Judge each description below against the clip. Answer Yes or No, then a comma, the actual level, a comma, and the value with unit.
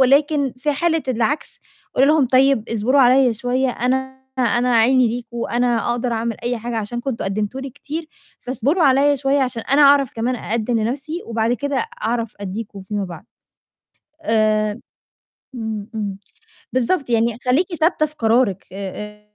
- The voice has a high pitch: Yes, high, 245 Hz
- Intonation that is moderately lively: Yes, average, 3.4 semitones